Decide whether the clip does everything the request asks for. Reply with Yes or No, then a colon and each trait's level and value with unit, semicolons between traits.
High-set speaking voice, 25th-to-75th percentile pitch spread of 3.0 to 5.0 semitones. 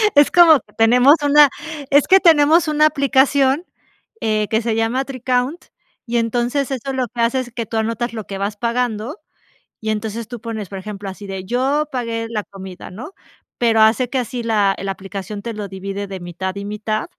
Yes: high, 230 Hz; average, 4.1 semitones